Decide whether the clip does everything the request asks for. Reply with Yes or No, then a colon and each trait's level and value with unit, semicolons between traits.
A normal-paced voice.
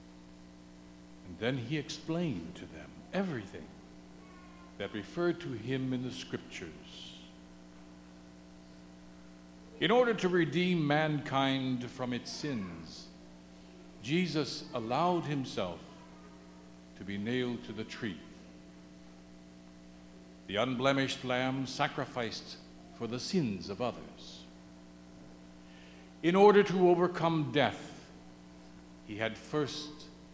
No: slow, 95 wpm